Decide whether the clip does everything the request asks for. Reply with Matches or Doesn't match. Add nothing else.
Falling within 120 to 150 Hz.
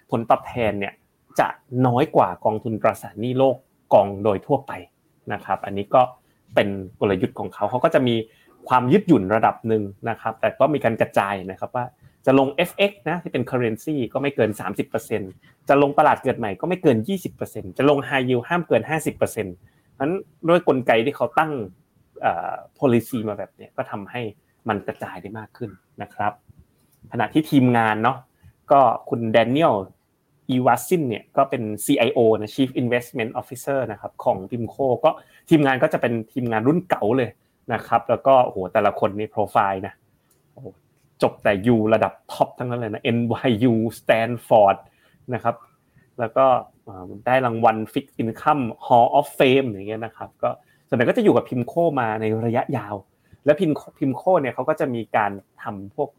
Matches